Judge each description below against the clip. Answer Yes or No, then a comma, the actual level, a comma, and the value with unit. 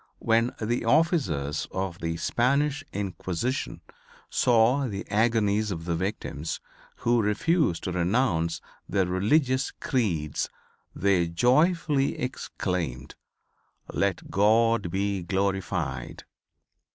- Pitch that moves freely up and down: Yes, wide, 5.9 semitones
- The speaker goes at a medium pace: No, slow, 95 wpm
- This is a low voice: Yes, low, 100 Hz